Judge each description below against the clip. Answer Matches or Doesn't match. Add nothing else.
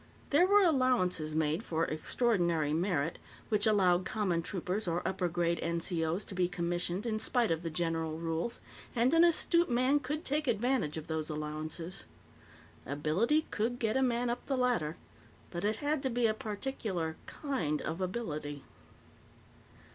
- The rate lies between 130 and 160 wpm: Matches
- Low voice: Doesn't match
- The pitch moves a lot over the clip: Matches